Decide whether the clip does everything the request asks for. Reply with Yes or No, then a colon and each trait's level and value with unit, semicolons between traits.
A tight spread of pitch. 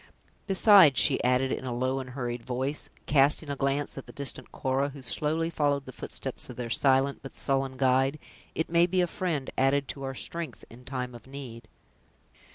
Yes: narrow, 2.1 semitones